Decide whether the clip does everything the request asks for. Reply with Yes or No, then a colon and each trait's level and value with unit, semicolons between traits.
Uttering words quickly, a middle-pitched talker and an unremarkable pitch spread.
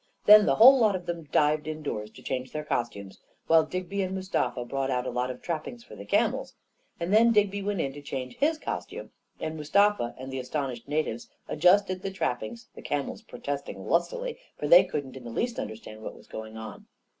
No: fast, 210 wpm; medium, 155 Hz; wide, 7.8 semitones